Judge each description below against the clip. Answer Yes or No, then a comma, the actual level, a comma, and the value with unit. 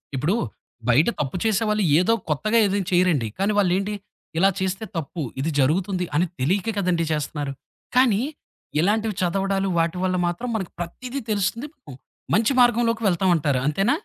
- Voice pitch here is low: No, high, 190 Hz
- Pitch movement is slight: No, average, 4.1 semitones